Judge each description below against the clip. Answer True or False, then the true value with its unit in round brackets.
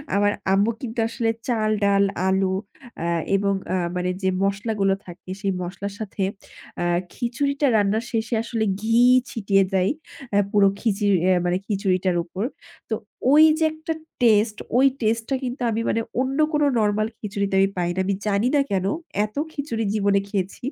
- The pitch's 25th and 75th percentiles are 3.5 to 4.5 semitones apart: False (2.8 semitones)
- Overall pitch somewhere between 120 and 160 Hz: False (205 Hz)